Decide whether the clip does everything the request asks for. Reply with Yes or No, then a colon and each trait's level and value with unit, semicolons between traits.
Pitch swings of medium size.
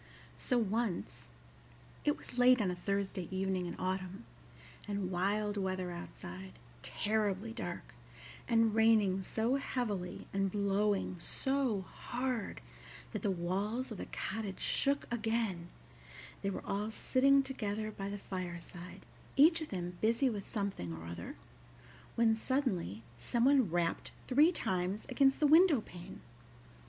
Yes: average, 4.4 semitones